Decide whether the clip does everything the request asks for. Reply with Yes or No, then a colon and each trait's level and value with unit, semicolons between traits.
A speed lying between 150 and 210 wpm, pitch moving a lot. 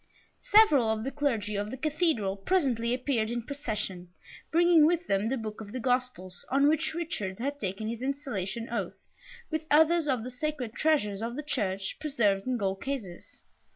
Yes: average, 175 wpm; wide, 6.0 semitones